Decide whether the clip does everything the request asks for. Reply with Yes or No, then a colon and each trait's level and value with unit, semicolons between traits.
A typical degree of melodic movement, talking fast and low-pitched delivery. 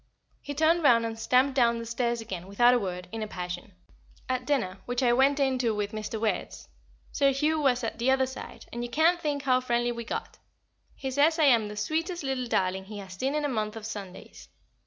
No: average, 4.2 semitones; fast, 225 wpm; high, 240 Hz